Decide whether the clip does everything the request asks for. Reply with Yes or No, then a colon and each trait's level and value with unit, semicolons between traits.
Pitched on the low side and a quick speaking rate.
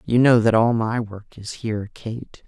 Yes: low, 110 Hz; fast, 220 wpm